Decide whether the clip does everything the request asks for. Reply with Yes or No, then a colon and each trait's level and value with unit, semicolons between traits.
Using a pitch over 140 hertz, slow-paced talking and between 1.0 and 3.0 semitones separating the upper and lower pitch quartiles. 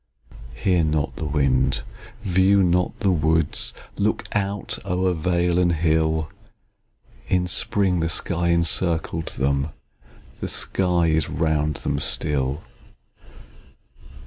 No: very low, 85 Hz; slow, 110 wpm; average, 2.7 semitones